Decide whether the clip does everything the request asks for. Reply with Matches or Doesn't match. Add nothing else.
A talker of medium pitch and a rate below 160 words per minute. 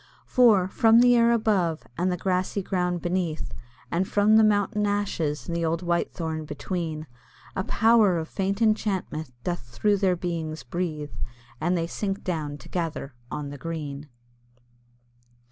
Matches